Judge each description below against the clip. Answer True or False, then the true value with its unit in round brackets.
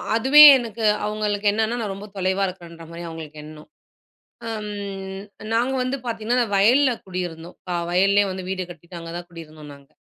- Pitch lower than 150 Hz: False (195 Hz)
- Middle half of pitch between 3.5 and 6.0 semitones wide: True (4.0 semitones)